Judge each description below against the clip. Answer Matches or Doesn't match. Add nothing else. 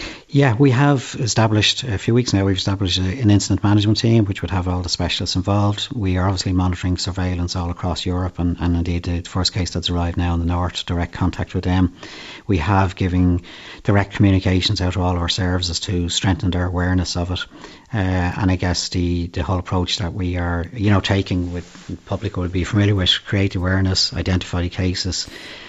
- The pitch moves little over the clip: Matches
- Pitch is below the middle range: Matches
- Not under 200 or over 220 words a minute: Matches